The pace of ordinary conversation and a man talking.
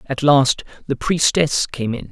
Yes: average, 170 wpm; male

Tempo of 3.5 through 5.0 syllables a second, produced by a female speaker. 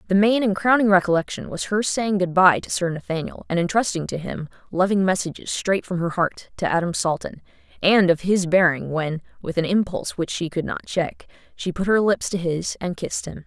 No: 5.4 syllables/s; female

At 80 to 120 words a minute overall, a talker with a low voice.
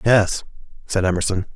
Yes: slow, 115 wpm; very low, 95 Hz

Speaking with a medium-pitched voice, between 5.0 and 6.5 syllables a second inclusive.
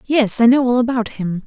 No: high, 235 Hz; 5.2 syllables/s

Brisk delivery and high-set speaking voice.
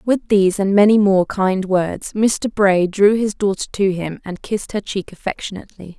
No: average, 190 wpm; high, 200 Hz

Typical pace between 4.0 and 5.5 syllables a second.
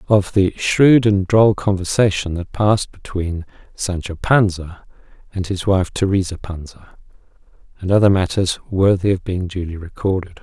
Yes: 4.7 syllables/s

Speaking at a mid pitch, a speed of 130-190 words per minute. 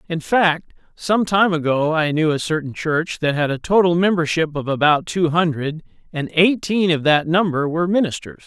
Yes: medium, 165 Hz; average, 185 wpm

